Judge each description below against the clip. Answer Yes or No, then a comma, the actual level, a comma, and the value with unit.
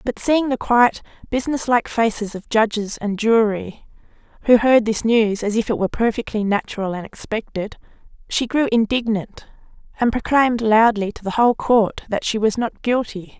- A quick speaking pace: No, average, 170 wpm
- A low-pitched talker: No, high, 225 Hz